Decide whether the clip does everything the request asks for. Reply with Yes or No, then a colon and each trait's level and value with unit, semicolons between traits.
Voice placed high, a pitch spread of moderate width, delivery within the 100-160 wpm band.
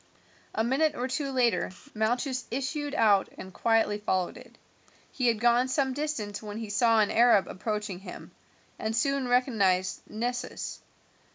Yes: high, 235 Hz; average, 3.5 semitones; average, 150 wpm